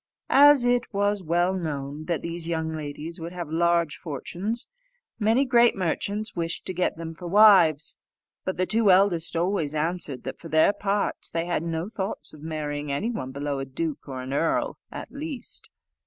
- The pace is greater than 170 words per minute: Yes, average, 180 wpm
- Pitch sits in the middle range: Yes, medium, 170 Hz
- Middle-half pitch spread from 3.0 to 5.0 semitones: Yes, average, 4.4 semitones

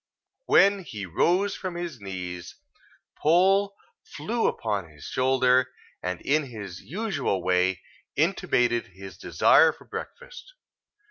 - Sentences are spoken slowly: Yes, slow, 115 wpm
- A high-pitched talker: No, low, 130 Hz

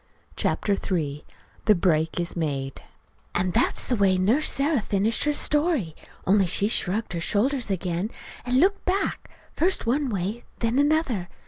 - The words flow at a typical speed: Yes, average, 150 wpm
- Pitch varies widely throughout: Yes, wide, 7.5 semitones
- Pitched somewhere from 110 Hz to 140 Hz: No, high, 210 Hz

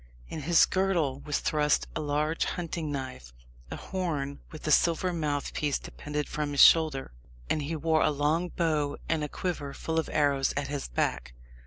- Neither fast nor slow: Yes, average, 175 wpm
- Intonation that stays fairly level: Yes, narrow, 2.3 semitones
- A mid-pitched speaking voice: Yes, medium, 150 Hz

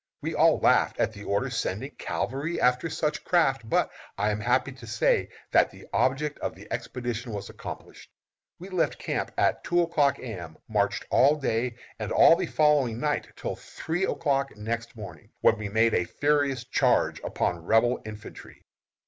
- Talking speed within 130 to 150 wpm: No, average, 175 wpm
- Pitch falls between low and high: No, low, 125 Hz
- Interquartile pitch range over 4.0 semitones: Yes, average, 5.2 semitones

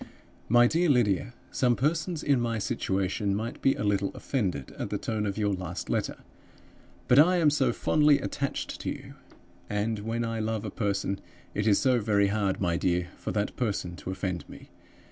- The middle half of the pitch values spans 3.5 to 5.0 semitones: Yes, average, 4.0 semitones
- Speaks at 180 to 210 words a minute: Yes, average, 185 wpm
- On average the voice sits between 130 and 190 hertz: No, low, 110 Hz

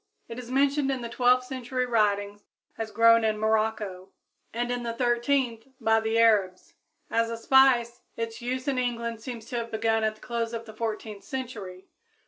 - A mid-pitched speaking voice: No, high, 230 Hz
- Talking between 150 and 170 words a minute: No, average, 180 wpm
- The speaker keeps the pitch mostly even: Yes, narrow, 2.0 semitones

